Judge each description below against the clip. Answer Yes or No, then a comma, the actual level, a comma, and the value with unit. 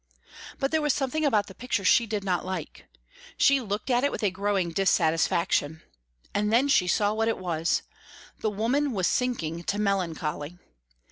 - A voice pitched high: Yes, high, 205 Hz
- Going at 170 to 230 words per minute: Yes, average, 175 wpm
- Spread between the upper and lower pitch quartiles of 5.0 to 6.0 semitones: Yes, wide, 5.4 semitones